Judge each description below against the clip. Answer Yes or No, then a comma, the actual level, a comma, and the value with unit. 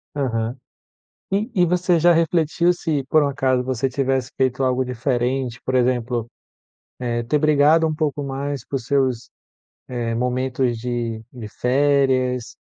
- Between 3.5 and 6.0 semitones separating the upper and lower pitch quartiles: No, average, 2.7 semitones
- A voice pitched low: Yes, low, 130 Hz